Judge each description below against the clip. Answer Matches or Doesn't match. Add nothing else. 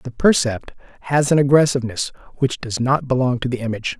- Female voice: Doesn't match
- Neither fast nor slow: Matches